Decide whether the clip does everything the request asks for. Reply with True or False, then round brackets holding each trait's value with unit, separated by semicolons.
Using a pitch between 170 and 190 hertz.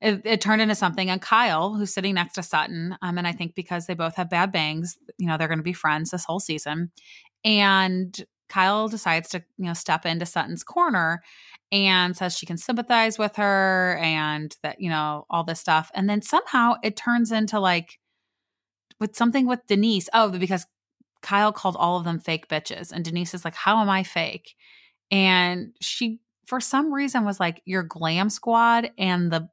True (185 Hz)